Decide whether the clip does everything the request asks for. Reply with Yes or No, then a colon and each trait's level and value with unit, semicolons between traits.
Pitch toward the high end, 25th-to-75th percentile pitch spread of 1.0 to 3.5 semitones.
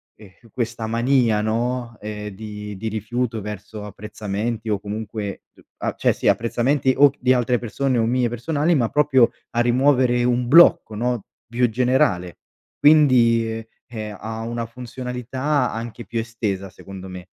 No: low, 115 Hz; average, 2.7 semitones